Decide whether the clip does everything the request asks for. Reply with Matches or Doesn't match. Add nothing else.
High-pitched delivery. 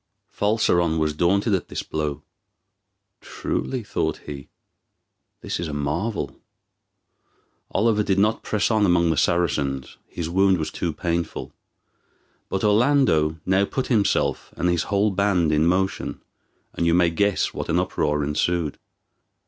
Doesn't match